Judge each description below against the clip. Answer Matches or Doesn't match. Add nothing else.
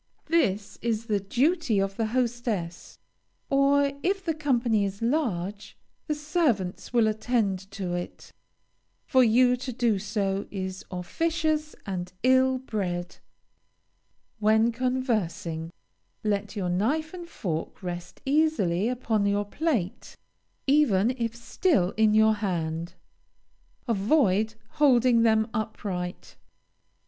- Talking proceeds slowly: Matches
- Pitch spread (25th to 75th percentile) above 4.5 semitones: Matches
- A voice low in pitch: Doesn't match